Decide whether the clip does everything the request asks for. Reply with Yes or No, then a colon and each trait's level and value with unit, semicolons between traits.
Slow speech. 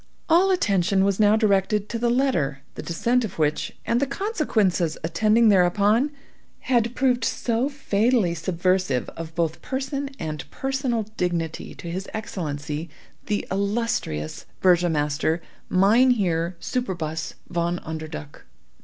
Yes: slow, 120 wpm